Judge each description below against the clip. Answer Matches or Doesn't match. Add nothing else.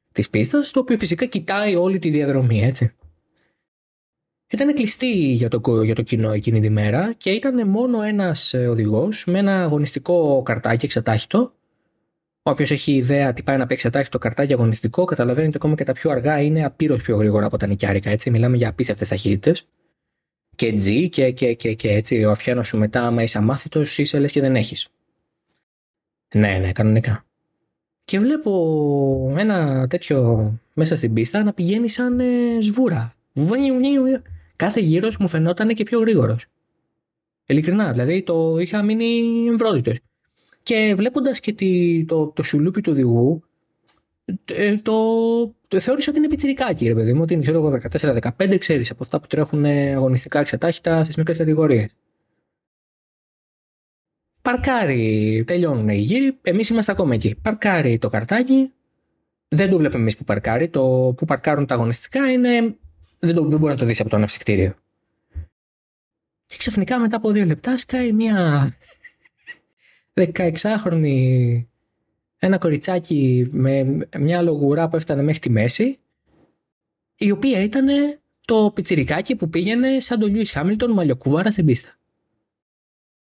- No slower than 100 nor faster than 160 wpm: Matches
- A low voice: Doesn't match